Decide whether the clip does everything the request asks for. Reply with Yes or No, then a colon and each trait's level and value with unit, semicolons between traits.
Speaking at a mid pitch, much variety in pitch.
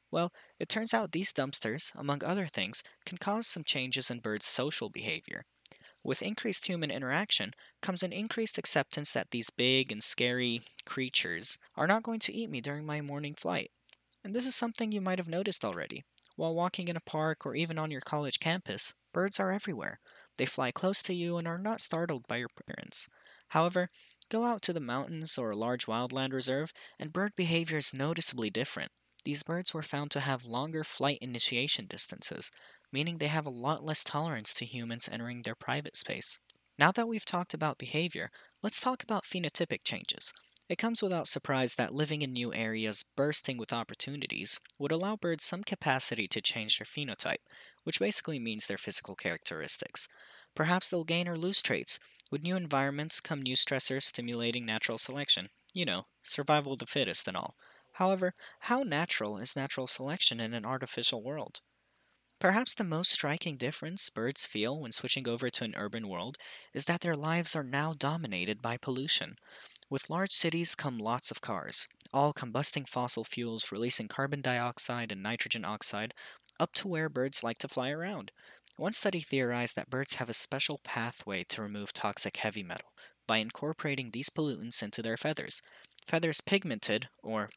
Yes: medium, 145 Hz; wide, 5.7 semitones